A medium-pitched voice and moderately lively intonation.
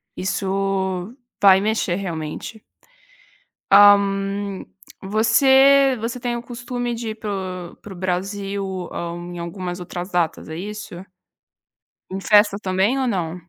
No: high, 195 Hz; average, 3.6 semitones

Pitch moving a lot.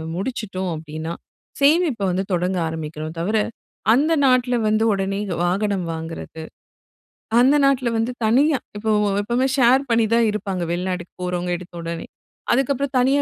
Yes: wide, 6.1 semitones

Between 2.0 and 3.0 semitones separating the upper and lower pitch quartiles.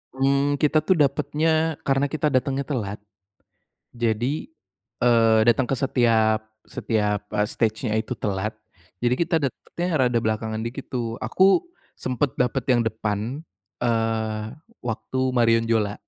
No: average, 3.6 semitones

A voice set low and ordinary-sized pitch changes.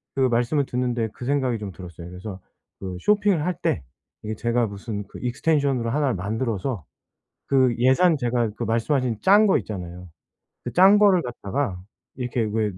Yes: low, 120 Hz; average, 5.0 semitones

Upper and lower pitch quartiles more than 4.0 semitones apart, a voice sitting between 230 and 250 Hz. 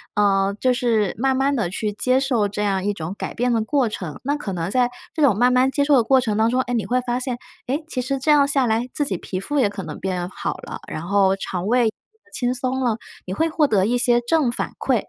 Yes: average, 4.5 semitones; high, 240 Hz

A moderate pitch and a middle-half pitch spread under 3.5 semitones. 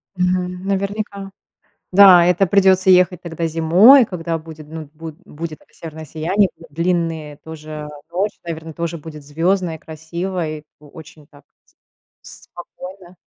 Yes: medium, 170 Hz; narrow, 2.6 semitones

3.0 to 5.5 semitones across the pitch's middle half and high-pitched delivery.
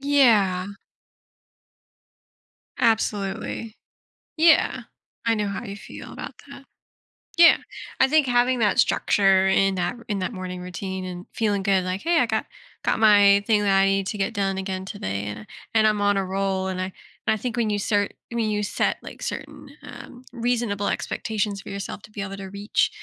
No: narrow, 2.5 semitones; high, 200 Hz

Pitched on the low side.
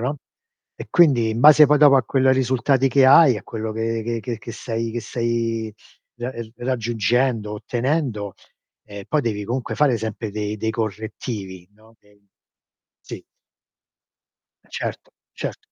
Yes: low, 115 Hz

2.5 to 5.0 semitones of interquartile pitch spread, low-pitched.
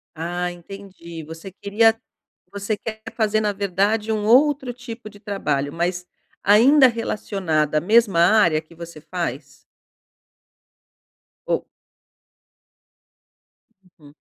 No: average, 4.5 semitones; high, 200 Hz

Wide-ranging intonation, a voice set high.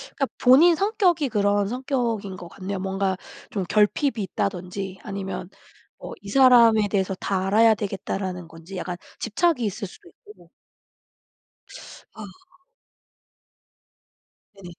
No: average, 4.5 semitones; high, 200 Hz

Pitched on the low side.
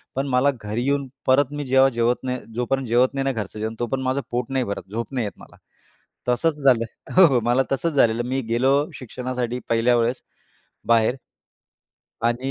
Yes: low, 125 Hz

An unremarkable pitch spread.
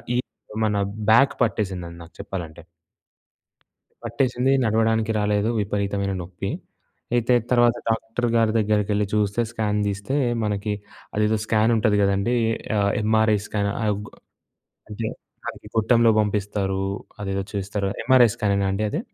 No: narrow, 1.9 semitones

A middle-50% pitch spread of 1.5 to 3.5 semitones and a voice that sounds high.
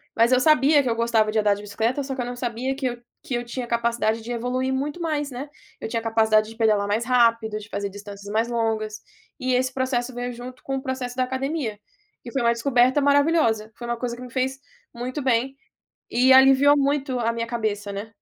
Yes: average, 2.8 semitones; high, 245 Hz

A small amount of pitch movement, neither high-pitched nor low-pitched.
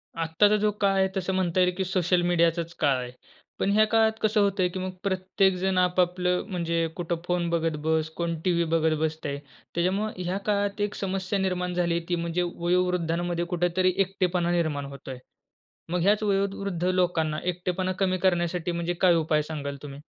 Yes: narrow, 2.1 semitones; medium, 180 Hz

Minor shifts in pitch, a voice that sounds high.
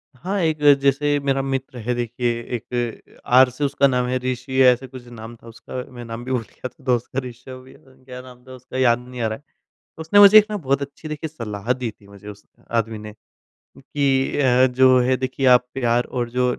No: narrow, 1.9 semitones; low, 125 Hz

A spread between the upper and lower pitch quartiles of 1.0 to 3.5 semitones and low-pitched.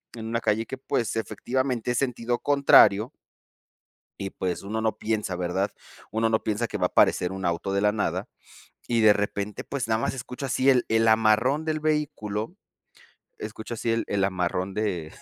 Yes: average, 3.2 semitones; low, 110 Hz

